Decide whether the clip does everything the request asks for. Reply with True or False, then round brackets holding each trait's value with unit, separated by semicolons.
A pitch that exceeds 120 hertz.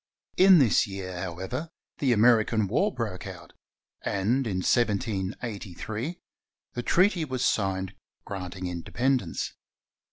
False (110 Hz)